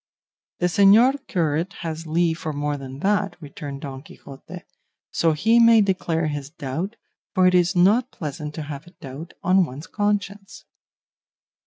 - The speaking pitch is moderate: Yes, medium, 170 Hz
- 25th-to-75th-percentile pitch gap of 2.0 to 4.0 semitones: No, average, 4.9 semitones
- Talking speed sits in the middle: Yes, average, 155 wpm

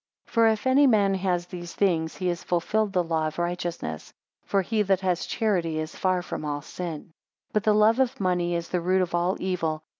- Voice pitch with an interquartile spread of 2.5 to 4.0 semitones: Yes, average, 2.8 semitones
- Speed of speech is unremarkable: No, fast, 220 wpm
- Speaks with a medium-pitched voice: Yes, medium, 180 Hz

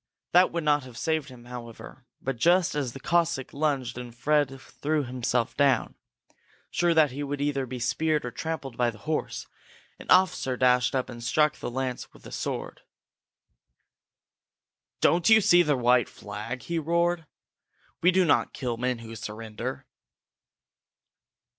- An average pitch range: Yes, average, 4.5 semitones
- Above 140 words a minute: Yes, average, 160 wpm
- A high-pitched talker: No, low, 135 Hz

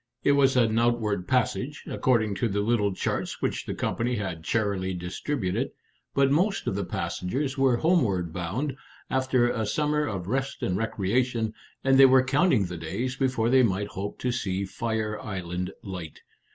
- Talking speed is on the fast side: No, average, 165 wpm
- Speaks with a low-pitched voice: Yes, low, 115 Hz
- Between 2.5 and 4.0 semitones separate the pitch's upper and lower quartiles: No, average, 5.2 semitones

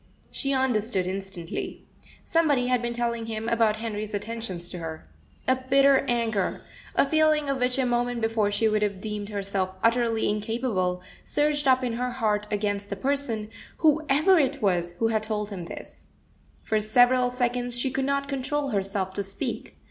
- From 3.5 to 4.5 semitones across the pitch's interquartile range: Yes, average, 4.0 semitones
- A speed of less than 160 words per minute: No, average, 170 wpm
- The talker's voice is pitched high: Yes, high, 230 Hz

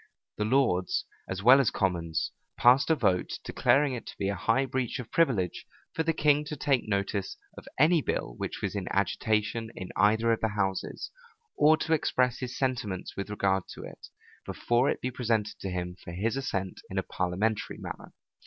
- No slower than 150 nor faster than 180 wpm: No, average, 190 wpm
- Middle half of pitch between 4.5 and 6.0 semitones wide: Yes, wide, 5.4 semitones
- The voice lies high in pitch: No, low, 110 Hz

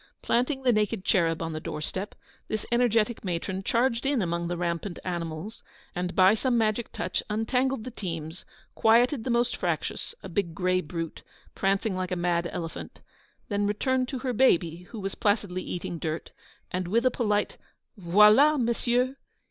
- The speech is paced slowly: No, average, 165 wpm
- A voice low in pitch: No, high, 205 Hz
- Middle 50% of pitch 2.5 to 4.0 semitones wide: No, average, 5.3 semitones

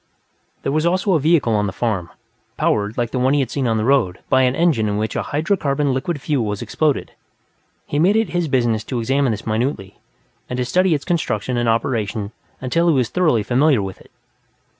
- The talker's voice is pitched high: No, low, 130 Hz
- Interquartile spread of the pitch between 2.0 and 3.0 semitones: No, wide, 5.6 semitones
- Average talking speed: No, fast, 210 wpm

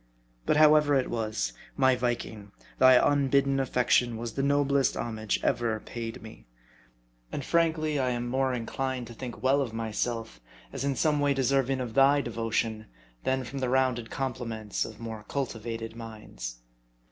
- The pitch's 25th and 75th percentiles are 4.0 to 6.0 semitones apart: No, average, 3.2 semitones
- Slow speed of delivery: No, average, 150 wpm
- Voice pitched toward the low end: Yes, low, 125 Hz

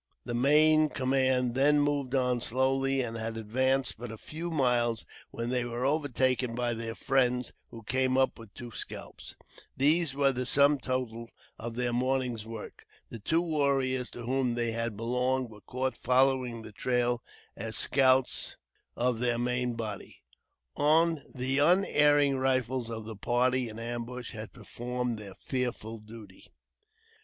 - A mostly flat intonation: Yes, narrow, 2.3 semitones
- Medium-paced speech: Yes, average, 150 wpm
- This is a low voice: Yes, low, 125 Hz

